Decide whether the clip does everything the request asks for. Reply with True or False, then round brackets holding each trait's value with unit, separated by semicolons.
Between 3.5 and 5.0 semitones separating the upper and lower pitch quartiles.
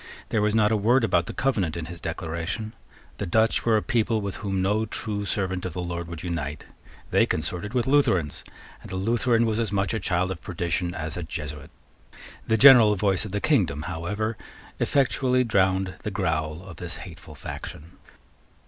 True (4.4 semitones)